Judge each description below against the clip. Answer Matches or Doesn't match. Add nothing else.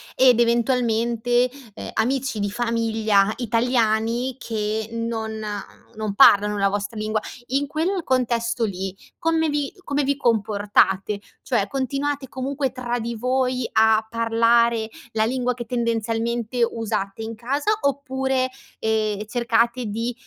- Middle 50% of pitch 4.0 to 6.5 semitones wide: Doesn't match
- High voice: Matches